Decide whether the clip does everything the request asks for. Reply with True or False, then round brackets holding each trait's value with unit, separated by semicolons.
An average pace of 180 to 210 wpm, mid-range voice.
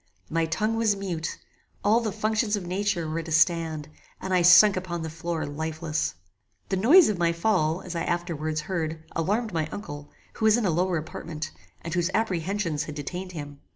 True (190 wpm; 170 Hz)